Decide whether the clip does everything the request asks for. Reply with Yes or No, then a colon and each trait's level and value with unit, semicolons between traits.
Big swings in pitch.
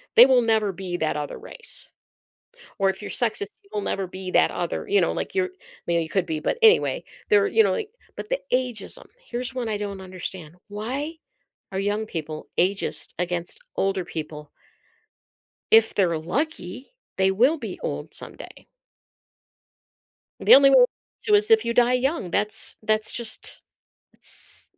Yes: wide, 6.2 semitones